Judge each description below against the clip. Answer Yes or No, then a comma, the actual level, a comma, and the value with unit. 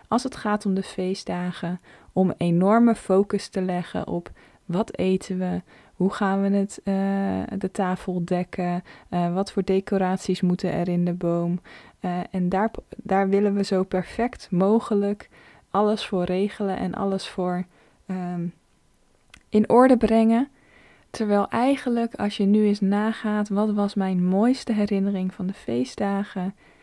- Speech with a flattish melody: Yes, narrow, 2.2 semitones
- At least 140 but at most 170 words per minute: Yes, average, 150 wpm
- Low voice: No, high, 195 Hz